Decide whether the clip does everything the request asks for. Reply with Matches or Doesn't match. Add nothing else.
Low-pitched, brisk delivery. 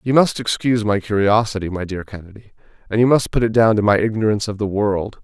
Matches